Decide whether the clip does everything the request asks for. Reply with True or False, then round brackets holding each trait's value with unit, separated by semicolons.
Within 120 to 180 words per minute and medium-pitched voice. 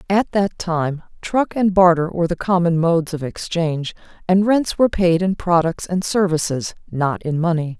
True (175 wpm; 175 Hz)